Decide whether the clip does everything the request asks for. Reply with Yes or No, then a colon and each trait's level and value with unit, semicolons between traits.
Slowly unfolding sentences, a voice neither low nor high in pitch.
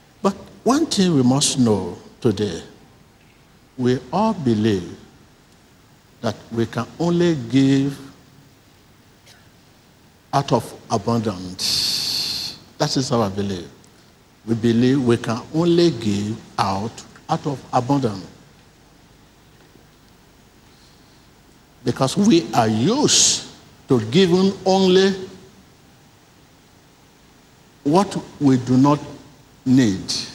No: slow, 85 wpm; low, 130 Hz